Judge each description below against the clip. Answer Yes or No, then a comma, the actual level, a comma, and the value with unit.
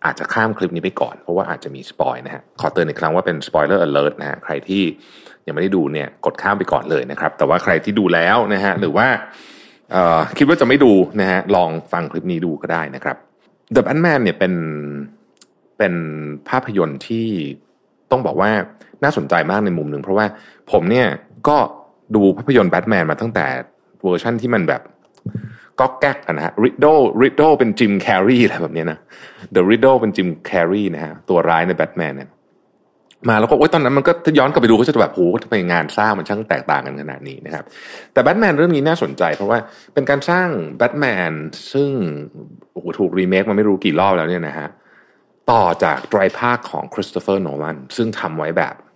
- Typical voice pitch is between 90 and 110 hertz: Yes, low, 100 Hz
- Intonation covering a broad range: Yes, wide, 5.8 semitones